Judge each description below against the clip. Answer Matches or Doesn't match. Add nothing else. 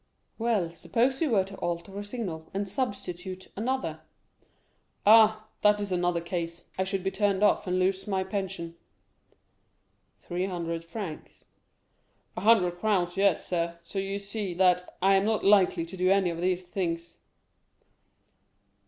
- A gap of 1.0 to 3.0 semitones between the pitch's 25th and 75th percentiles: Matches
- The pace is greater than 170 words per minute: Doesn't match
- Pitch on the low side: Doesn't match